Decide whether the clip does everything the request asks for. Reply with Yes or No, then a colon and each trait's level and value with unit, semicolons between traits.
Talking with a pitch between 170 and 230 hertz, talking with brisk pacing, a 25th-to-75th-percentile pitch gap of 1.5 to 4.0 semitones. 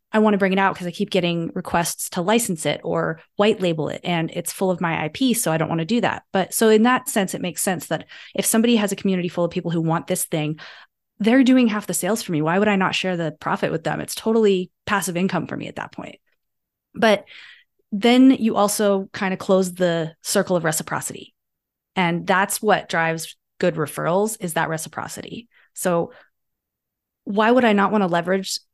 Yes: high, 190 Hz; fast, 220 wpm; average, 3.4 semitones